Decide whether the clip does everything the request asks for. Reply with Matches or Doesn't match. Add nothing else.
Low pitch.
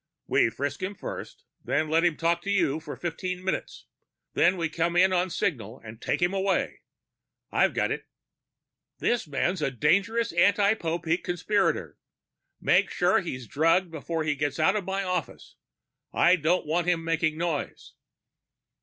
Doesn't match